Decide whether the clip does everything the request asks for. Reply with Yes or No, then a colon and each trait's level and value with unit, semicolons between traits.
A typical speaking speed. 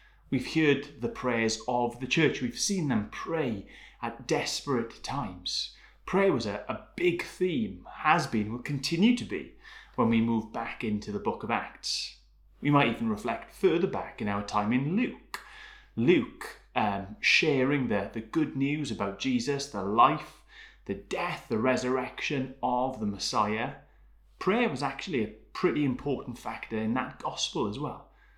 Yes: average, 160 wpm